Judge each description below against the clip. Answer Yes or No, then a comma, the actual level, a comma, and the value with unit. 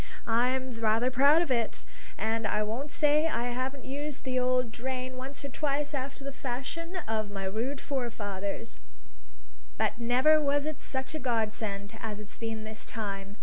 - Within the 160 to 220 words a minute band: Yes, average, 165 wpm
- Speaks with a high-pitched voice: Yes, very high, 250 Hz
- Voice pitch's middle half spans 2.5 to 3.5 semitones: No, average, 3.9 semitones